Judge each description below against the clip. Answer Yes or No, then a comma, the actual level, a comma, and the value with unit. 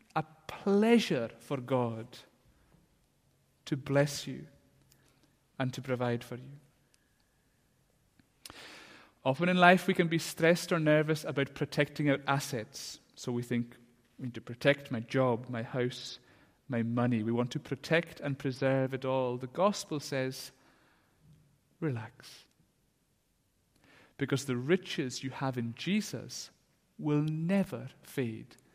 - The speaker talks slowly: Yes, slow, 125 wpm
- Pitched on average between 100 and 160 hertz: Yes, low, 135 Hz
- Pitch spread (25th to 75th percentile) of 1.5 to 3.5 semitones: No, average, 3.9 semitones